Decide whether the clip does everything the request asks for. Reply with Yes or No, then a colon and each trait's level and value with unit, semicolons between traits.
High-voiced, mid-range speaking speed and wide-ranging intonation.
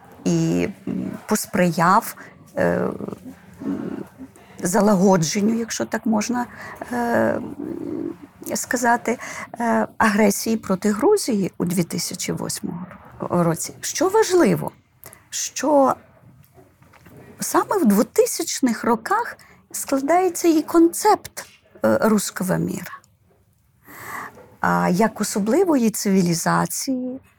No: high, 230 Hz; slow, 65 wpm; wide, 7.4 semitones